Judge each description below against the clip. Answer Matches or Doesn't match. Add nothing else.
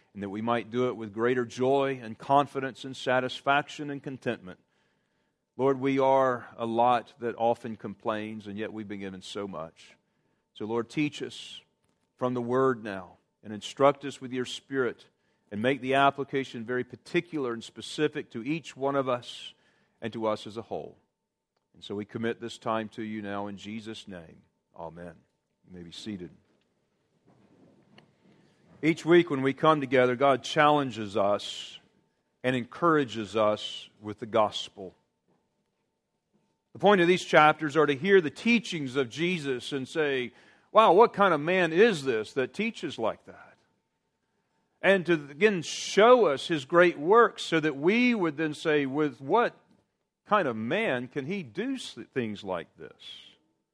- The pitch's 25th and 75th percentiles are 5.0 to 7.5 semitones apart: Matches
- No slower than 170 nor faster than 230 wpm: Doesn't match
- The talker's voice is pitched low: Matches